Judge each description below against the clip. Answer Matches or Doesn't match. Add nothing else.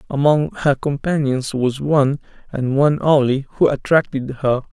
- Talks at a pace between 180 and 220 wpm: Doesn't match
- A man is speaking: Matches